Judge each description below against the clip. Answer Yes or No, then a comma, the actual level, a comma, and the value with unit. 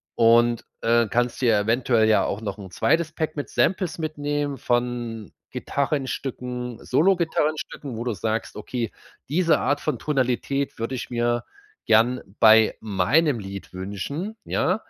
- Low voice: Yes, low, 120 Hz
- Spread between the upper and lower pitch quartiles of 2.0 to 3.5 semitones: No, average, 4.5 semitones